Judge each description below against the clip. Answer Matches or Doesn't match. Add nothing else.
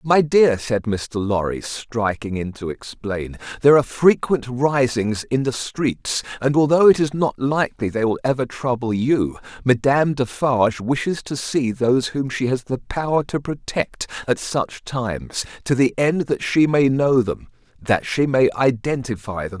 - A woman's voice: Doesn't match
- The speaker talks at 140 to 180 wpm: Matches